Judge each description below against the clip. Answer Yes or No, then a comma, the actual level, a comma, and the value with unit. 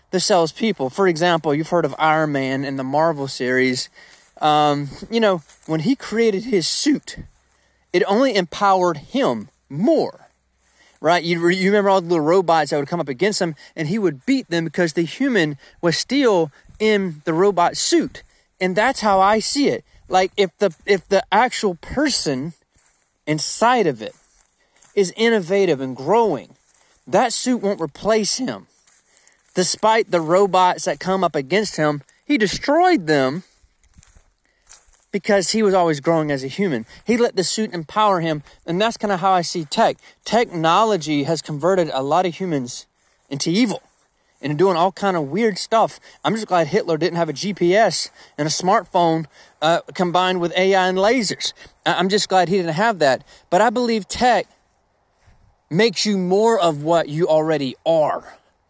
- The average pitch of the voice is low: No, medium, 180 Hz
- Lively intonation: No, average, 4.6 semitones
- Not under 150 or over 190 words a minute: Yes, average, 170 wpm